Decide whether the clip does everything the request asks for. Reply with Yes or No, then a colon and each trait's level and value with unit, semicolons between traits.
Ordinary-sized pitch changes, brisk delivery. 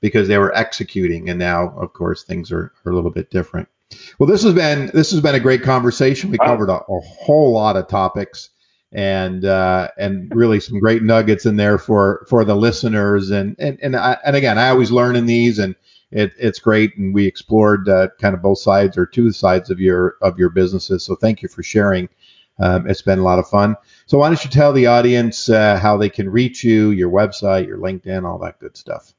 Yes: average, 3.9 semitones; fast, 225 wpm